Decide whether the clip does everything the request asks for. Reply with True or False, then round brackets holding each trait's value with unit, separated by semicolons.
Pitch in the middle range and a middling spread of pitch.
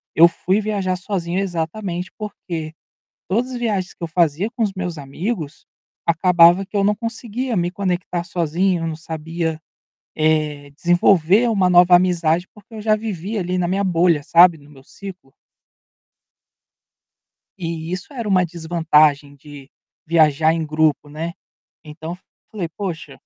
True (175 Hz; 3.5 semitones)